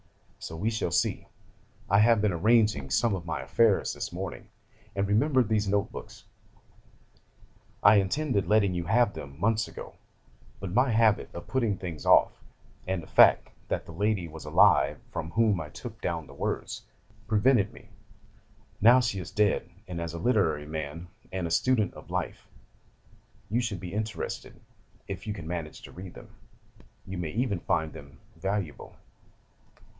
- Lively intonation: No, average, 4.6 semitones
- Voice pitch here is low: Yes, low, 100 Hz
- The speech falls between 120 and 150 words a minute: No, average, 160 wpm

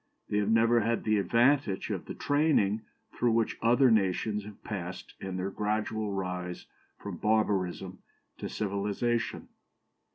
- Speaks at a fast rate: No, slow, 135 wpm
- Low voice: Yes, low, 105 Hz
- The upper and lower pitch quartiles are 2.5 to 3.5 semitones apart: Yes, average, 3.0 semitones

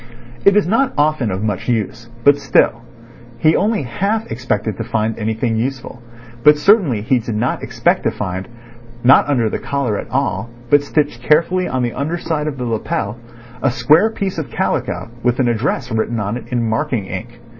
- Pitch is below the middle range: Yes, low, 120 Hz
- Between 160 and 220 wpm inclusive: Yes, average, 175 wpm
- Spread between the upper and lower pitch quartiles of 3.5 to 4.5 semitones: Yes, average, 4.2 semitones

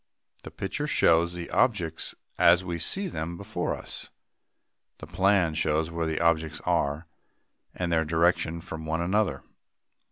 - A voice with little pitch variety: Yes, narrow, 2.1 semitones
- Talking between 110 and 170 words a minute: Yes, average, 150 wpm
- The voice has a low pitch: Yes, very low, 85 Hz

